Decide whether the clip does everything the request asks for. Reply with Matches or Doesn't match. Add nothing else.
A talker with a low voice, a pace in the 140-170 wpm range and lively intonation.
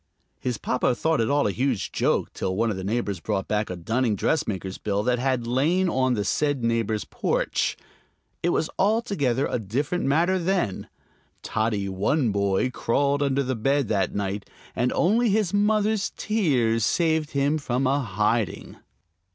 Matches